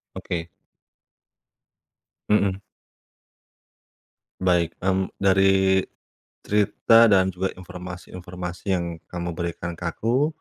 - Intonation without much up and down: Yes, narrow, 1.7 semitones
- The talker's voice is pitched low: Yes, very low, 90 Hz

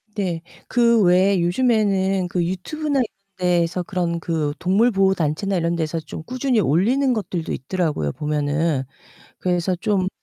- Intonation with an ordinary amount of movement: Yes, average, 3.5 semitones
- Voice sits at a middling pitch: Yes, medium, 180 Hz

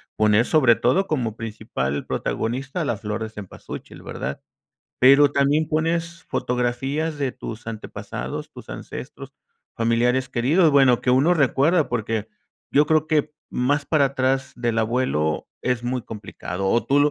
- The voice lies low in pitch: Yes, low, 130 Hz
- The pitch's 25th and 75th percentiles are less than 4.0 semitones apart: No, average, 4.3 semitones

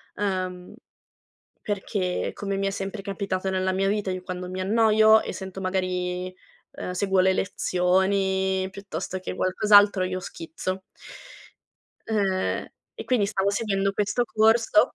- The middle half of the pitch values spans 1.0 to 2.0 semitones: Yes, narrow, 1.6 semitones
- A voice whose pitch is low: No, high, 190 Hz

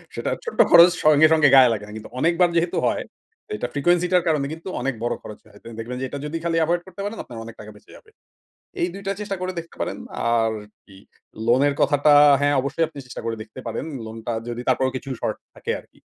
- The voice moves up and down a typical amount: No, wide, 6.0 semitones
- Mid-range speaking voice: Yes, medium, 145 Hz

